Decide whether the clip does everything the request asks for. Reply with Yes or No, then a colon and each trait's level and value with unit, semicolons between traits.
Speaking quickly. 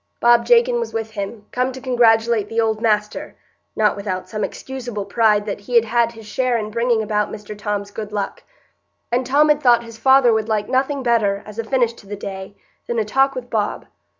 Yes: fast, 210 wpm